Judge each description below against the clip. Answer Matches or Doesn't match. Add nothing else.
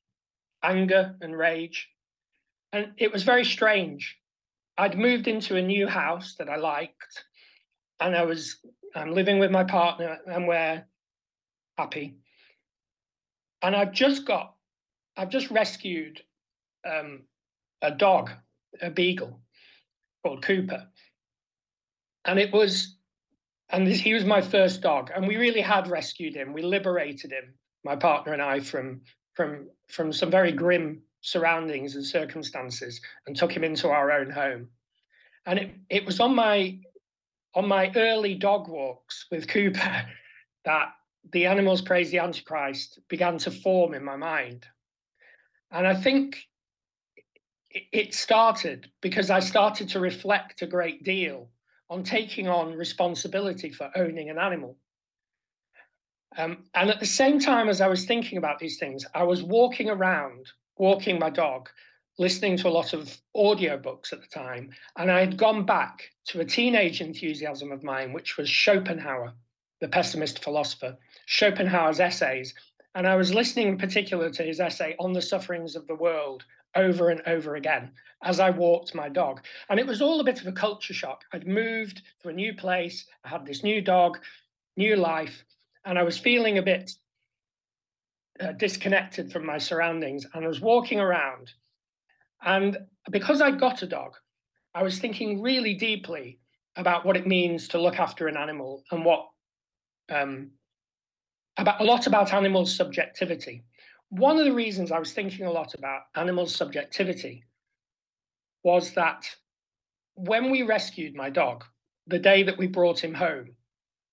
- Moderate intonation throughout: Matches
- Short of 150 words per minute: Doesn't match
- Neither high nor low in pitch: Matches